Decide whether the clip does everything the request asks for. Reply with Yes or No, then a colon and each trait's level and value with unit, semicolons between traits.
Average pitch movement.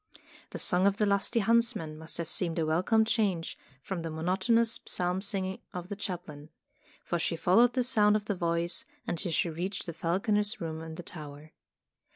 Yes: average, 4.0 semitones